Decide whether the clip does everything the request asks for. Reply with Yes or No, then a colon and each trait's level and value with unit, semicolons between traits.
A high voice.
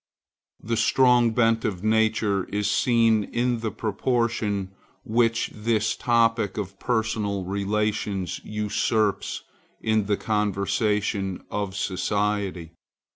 No: low, 105 Hz